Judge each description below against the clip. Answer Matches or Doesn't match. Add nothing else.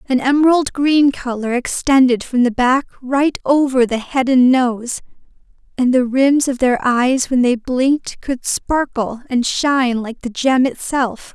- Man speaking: Doesn't match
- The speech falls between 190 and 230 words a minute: Doesn't match